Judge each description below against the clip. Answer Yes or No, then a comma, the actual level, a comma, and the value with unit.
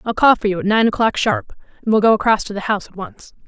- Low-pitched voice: No, high, 215 Hz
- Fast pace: Yes, fast, 295 wpm